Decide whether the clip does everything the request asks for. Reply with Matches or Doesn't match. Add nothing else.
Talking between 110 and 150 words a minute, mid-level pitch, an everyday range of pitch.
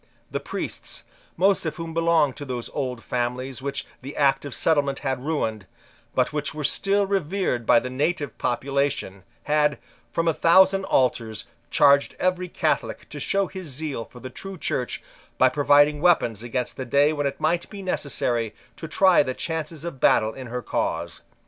Doesn't match